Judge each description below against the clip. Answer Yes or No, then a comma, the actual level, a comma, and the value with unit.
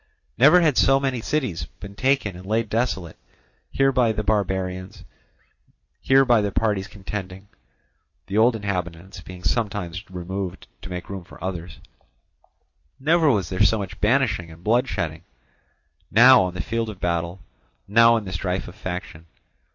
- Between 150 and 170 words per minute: Yes, average, 155 wpm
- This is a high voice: No, low, 100 Hz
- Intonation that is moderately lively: Yes, average, 4.1 semitones